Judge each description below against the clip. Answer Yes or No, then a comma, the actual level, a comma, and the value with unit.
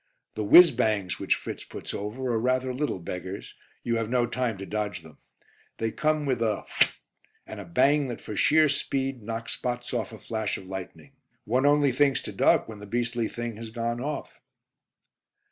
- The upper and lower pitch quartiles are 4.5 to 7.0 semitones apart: No, average, 3.5 semitones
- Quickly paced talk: No, average, 190 wpm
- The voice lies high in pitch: No, low, 115 Hz